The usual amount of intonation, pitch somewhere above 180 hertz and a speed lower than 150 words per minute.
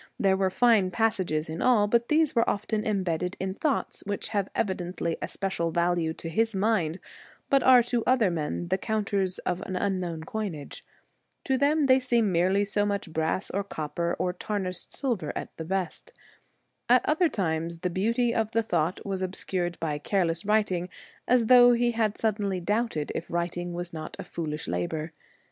No: average, 4.6 semitones; high, 190 Hz; average, 180 wpm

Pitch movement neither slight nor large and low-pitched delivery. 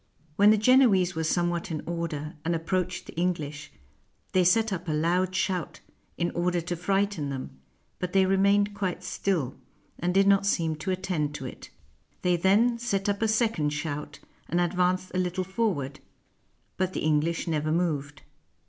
No: average, 3.2 semitones; medium, 180 Hz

